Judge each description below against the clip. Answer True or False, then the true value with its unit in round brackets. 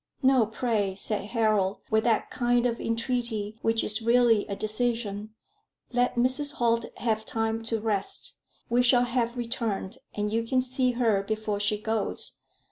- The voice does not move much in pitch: True (2.2 semitones)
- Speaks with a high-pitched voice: True (225 Hz)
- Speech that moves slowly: False (155 wpm)